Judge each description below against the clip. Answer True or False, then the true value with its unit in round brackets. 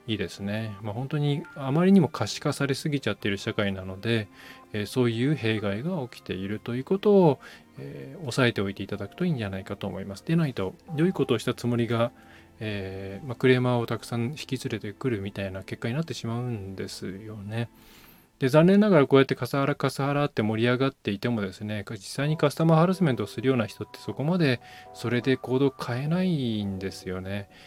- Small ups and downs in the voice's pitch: False (5.1 semitones)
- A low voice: True (120 Hz)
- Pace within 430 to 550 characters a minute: True (450 characters per minute)